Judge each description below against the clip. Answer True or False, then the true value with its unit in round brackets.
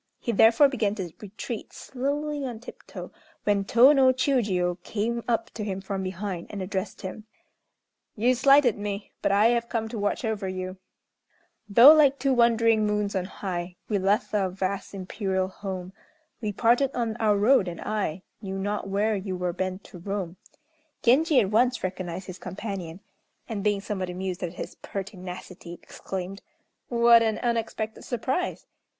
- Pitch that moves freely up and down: False (3.8 semitones)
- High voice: True (205 Hz)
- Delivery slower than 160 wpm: False (165 wpm)